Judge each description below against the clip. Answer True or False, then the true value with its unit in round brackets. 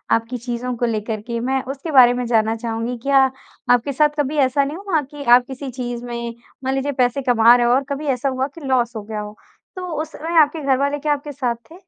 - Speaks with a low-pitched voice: False (255 Hz)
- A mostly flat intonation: False (3.0 semitones)